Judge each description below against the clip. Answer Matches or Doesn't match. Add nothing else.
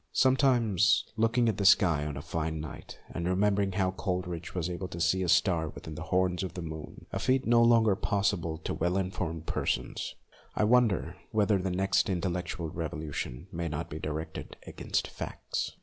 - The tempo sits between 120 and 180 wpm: Doesn't match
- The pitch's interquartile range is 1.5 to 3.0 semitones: Doesn't match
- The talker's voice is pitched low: Matches